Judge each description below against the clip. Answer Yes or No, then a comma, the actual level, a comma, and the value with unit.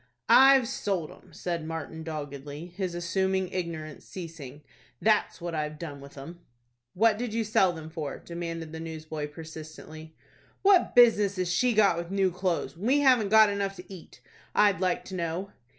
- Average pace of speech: Yes, average, 170 wpm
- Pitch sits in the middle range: Yes, medium, 175 Hz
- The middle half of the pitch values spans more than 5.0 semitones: No, average, 4.0 semitones